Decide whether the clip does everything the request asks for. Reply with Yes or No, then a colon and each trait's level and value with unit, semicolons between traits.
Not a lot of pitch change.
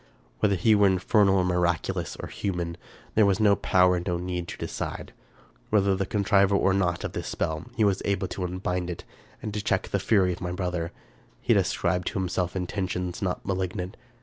Yes: narrow, 1.9 semitones